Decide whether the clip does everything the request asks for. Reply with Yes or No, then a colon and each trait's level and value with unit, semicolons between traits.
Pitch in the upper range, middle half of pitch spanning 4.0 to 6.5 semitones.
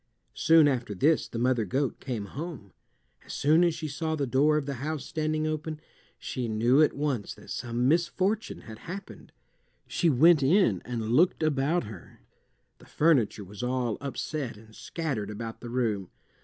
No: medium, 140 Hz; average, 5.1 semitones